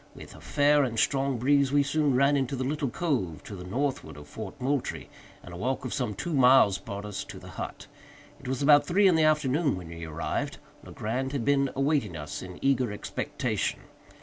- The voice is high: No, low, 130 Hz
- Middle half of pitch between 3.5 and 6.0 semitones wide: Yes, wide, 5.6 semitones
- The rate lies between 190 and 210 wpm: Yes, fast, 205 wpm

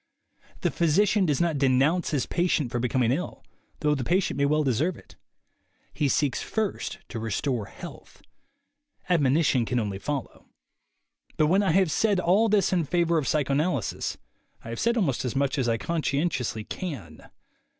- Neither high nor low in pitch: Yes, medium, 150 Hz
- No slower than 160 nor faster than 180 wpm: Yes, average, 170 wpm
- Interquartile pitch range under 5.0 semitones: No, wide, 5.5 semitones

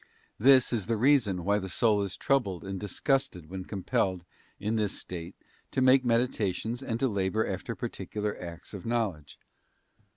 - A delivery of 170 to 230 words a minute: No, average, 160 wpm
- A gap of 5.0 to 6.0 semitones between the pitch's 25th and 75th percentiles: No, average, 4.0 semitones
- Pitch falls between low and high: No, low, 105 Hz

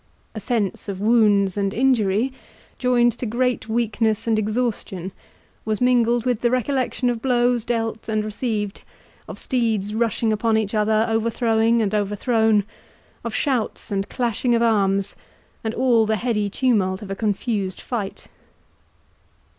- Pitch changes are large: No, narrow, 2.5 semitones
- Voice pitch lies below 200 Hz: No, high, 225 Hz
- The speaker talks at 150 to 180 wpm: No, average, 140 wpm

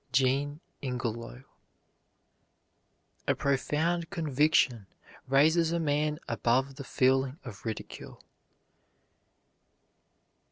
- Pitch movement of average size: Yes, average, 3.1 semitones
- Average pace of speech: No, slow, 75 wpm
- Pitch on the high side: No, medium, 140 Hz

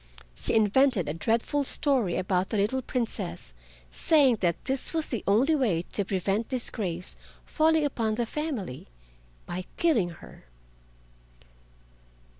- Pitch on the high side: Yes, high, 220 Hz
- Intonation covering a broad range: Yes, wide, 6.9 semitones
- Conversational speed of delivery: No, slow, 120 wpm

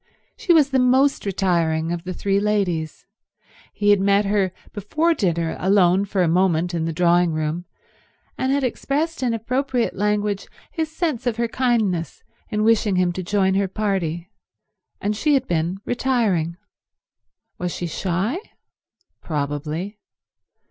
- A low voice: No, high, 200 Hz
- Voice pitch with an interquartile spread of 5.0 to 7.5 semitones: Yes, average, 5.3 semitones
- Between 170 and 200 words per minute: No, average, 145 wpm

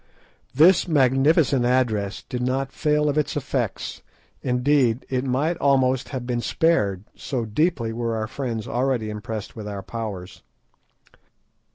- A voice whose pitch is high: No, low, 125 Hz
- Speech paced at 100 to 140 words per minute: Yes, slow, 135 wpm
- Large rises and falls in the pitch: No, average, 3.8 semitones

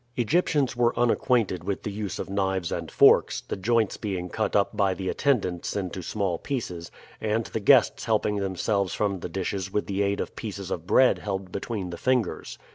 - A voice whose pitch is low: Yes, low, 100 Hz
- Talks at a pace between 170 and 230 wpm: Yes, average, 190 wpm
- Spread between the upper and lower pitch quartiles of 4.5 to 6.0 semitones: No, average, 3.1 semitones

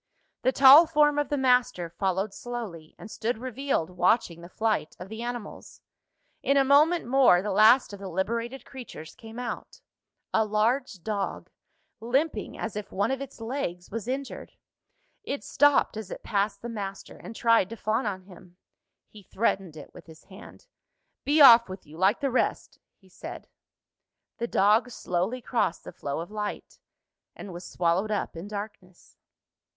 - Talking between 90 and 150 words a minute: No, average, 165 wpm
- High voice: Yes, high, 215 Hz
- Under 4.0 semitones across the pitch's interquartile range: No, average, 4.8 semitones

